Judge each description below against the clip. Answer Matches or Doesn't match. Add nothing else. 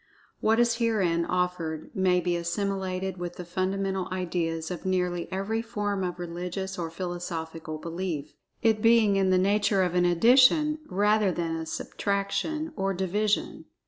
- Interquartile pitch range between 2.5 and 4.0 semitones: Matches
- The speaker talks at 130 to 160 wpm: Matches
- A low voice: Doesn't match